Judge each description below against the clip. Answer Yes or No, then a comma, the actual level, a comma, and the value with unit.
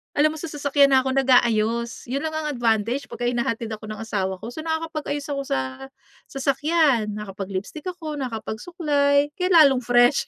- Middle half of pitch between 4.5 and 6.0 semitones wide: Yes, average, 4.8 semitones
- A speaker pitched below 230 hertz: No, very high, 270 Hz